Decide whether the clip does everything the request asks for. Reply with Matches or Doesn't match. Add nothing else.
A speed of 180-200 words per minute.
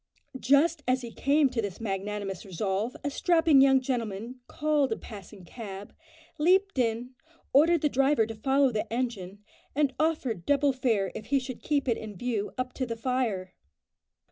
Doesn't match